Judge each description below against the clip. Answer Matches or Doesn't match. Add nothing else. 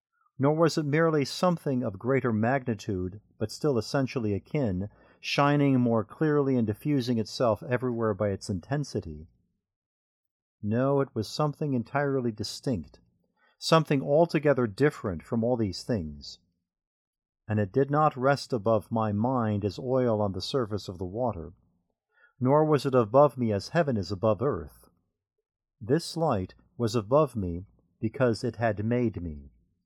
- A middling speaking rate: Matches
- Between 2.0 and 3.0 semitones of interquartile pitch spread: Doesn't match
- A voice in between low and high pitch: Doesn't match